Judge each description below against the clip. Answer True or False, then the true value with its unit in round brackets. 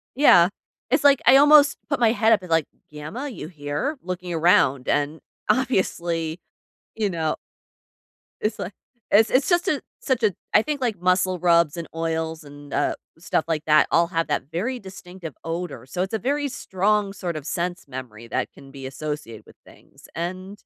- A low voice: False (180 Hz)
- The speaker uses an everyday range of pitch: False (5.9 semitones)